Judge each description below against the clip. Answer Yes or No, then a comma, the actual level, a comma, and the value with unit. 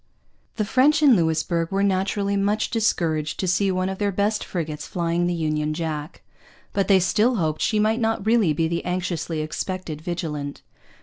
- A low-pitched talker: No, medium, 185 Hz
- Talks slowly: No, average, 175 wpm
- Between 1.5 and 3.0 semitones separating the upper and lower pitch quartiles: No, average, 4.1 semitones